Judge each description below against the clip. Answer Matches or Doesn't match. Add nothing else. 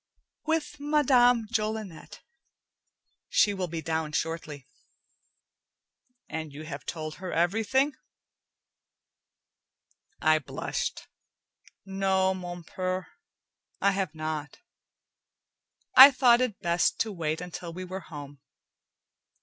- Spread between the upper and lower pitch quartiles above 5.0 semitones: Matches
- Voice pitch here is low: Doesn't match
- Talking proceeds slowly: Matches